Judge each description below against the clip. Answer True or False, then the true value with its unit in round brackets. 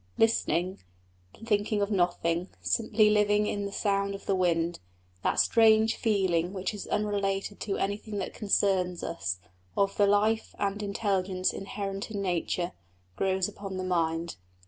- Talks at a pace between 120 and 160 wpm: True (145 wpm)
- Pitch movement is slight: True (2.2 semitones)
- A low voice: False (195 Hz)